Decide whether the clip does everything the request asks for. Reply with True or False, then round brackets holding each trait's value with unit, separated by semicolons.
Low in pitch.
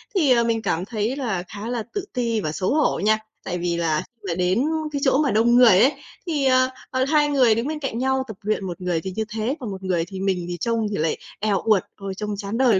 False (215 Hz)